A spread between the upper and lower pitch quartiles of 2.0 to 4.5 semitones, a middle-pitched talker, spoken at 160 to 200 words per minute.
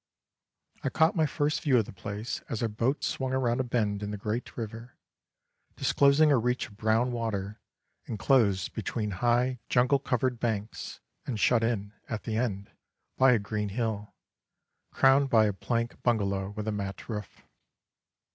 No: average, 3.2 semitones; low, 115 Hz; average, 165 wpm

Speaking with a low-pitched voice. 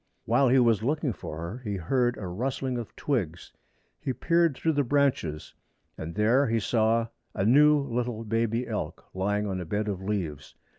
Yes: low, 115 Hz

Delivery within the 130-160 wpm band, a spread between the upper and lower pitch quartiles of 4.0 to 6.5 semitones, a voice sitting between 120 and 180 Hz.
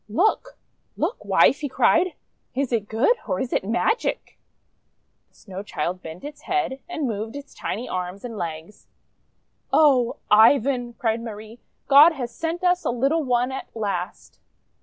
No: average, 155 wpm; wide, 5.5 semitones; high, 240 Hz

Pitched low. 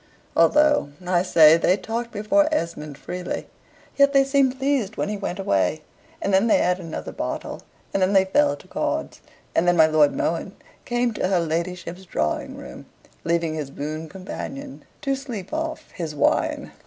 No: medium, 185 Hz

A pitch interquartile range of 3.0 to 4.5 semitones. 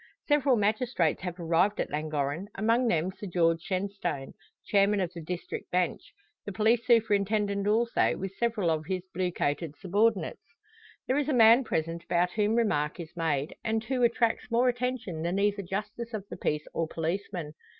No: average, 4.9 semitones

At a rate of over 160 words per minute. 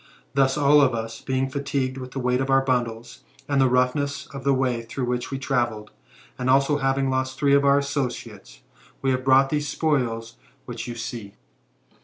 Yes: average, 190 wpm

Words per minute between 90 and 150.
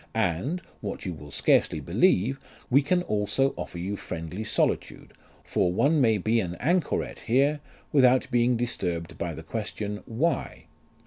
Yes: average, 145 wpm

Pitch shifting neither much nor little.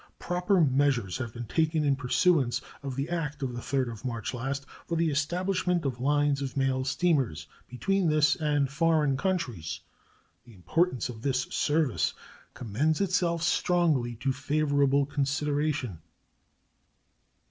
Yes: average, 3.9 semitones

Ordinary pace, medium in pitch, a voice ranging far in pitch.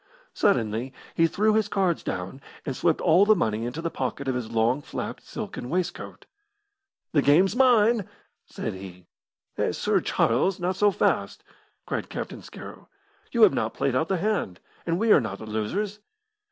Yes: average, 170 wpm; medium, 165 Hz; wide, 9.0 semitones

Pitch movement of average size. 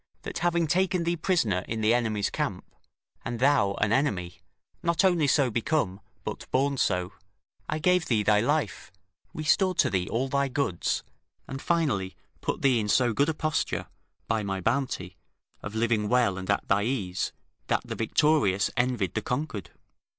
No: wide, 6.6 semitones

